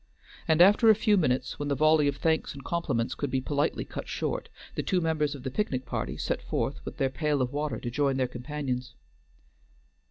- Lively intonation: No, average, 3.6 semitones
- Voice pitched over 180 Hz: No, medium, 145 Hz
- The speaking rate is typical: No, fast, 210 wpm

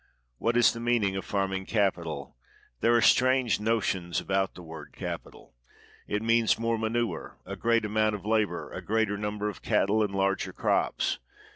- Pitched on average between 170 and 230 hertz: No, low, 105 Hz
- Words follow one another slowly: No, average, 165 wpm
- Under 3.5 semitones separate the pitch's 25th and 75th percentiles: Yes, average, 2.9 semitones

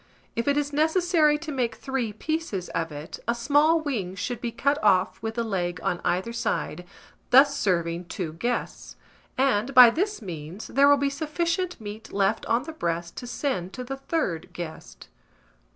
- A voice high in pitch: Yes, high, 235 Hz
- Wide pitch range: Yes, wide, 7.6 semitones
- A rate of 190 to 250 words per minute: No, average, 175 wpm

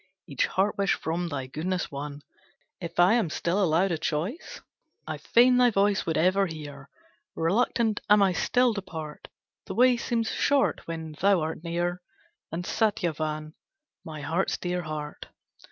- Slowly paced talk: No, average, 155 wpm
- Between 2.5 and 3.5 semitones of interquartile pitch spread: No, average, 4.5 semitones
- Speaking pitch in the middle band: Yes, medium, 175 Hz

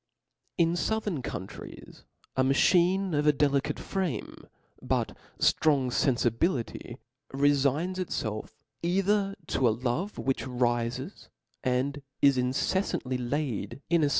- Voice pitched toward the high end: No, medium, 140 Hz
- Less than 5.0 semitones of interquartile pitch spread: No, wide, 5.5 semitones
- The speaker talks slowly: Yes, slow, 110 wpm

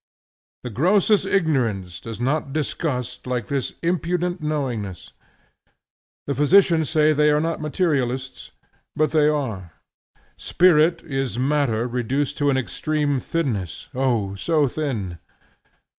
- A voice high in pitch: No, medium, 140 Hz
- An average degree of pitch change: Yes, average, 4.0 semitones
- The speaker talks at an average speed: No, slow, 115 wpm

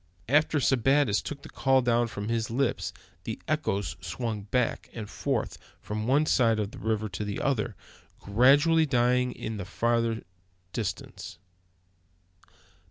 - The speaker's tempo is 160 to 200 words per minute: No, average, 145 wpm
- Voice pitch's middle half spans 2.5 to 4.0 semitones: Yes, average, 3.7 semitones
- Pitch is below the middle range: Yes, low, 115 Hz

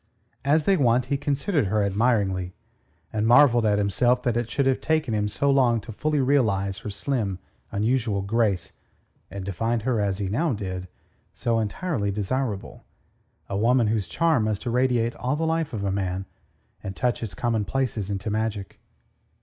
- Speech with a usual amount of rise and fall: Yes, average, 4.5 semitones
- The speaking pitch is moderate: No, low, 115 Hz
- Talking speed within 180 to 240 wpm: No, average, 170 wpm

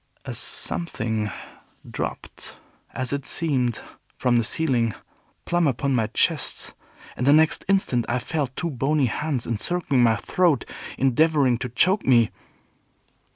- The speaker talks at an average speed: No, slow, 130 wpm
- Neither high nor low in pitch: No, low, 130 Hz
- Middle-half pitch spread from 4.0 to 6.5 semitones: Yes, average, 4.9 semitones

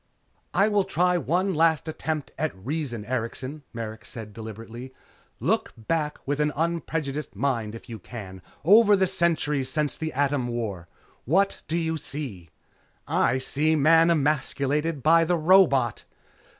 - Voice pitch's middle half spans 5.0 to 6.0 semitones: Yes, wide, 5.6 semitones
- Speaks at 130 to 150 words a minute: Yes, average, 140 wpm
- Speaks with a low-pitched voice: No, medium, 145 Hz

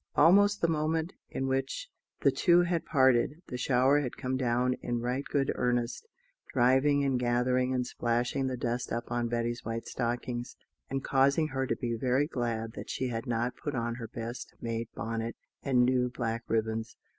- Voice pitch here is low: Yes, low, 125 Hz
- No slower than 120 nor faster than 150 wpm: No, average, 180 wpm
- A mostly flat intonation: Yes, narrow, 2.3 semitones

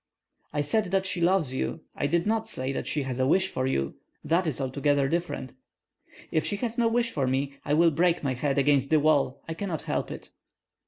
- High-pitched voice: No, medium, 150 Hz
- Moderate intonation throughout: Yes, average, 4.8 semitones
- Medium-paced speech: No, fast, 220 wpm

